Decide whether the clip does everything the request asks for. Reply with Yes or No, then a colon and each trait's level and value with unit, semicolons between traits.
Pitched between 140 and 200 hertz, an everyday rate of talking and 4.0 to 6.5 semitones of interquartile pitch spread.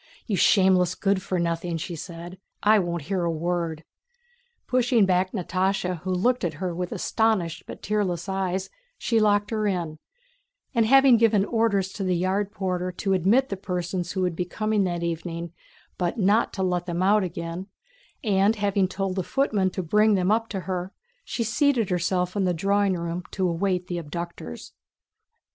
No: medium, 185 Hz; average, 175 wpm; average, 2.7 semitones